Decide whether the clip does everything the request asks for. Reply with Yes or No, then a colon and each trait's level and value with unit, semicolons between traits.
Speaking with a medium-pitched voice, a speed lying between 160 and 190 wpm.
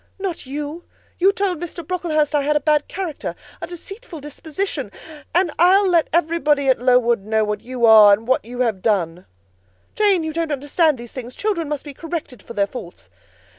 No: very high, 295 Hz; average, 185 wpm